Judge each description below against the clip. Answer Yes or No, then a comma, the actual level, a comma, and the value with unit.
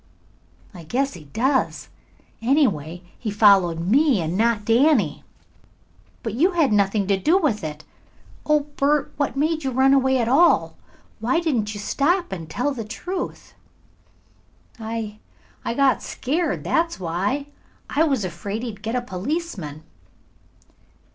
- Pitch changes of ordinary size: No, wide, 6.4 semitones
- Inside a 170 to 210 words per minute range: No, average, 140 wpm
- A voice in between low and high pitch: No, high, 235 Hz